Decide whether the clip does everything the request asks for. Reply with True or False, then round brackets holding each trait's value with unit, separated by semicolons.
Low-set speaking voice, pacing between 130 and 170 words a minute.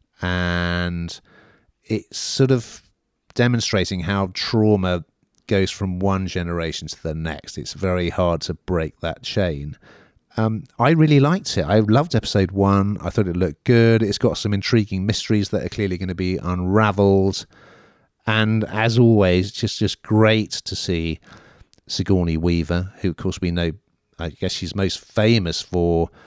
True (95 Hz; 160 wpm)